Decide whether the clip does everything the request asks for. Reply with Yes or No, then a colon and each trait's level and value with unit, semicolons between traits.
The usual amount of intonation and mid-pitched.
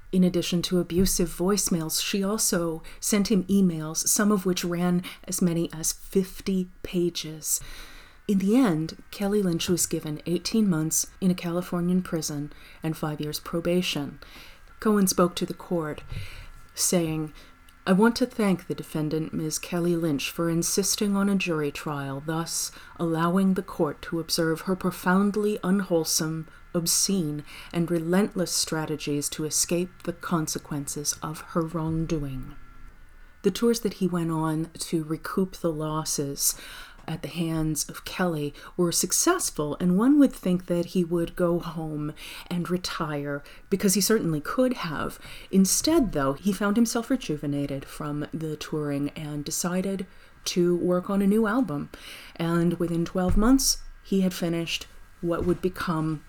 Yes: average, 3.3 semitones; medium, 170 Hz